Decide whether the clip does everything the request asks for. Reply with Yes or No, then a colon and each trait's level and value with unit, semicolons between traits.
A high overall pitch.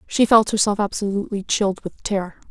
Yes: high, 205 Hz